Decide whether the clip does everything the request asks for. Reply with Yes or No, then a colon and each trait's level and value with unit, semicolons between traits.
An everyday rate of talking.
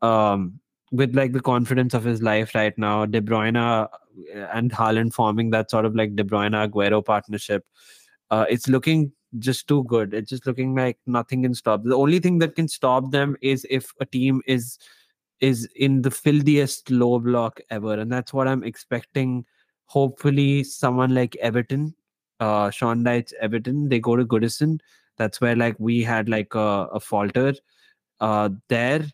Yes: average, 170 wpm